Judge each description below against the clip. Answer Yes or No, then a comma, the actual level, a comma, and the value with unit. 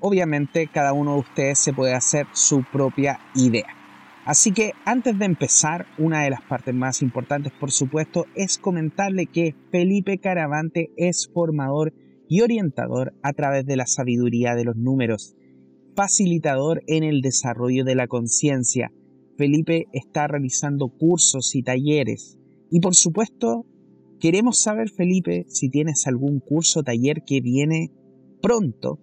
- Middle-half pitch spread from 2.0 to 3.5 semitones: No, average, 4.6 semitones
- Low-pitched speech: No, medium, 145 Hz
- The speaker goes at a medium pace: Yes, average, 140 wpm